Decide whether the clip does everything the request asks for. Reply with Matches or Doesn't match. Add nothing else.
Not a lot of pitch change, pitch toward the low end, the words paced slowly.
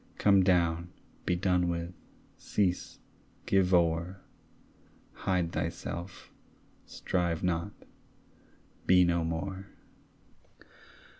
Matches